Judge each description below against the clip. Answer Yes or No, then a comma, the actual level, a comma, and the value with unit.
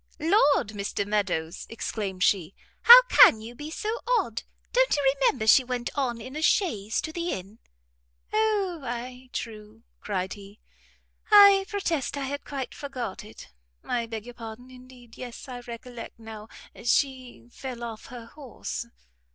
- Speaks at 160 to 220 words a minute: No, average, 150 wpm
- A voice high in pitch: Yes, high, 245 Hz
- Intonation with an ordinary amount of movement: Yes, average, 4.6 semitones